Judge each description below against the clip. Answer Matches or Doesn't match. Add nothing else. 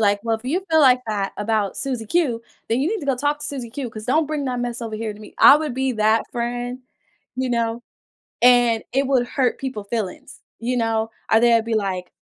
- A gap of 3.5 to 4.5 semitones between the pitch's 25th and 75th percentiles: Doesn't match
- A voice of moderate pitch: Doesn't match